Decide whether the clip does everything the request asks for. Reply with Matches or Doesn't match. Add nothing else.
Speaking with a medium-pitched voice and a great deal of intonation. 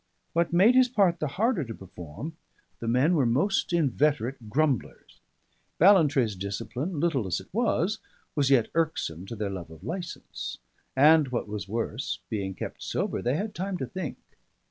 Matches